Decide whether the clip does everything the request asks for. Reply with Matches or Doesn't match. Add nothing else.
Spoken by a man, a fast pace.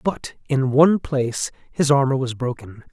Doesn't match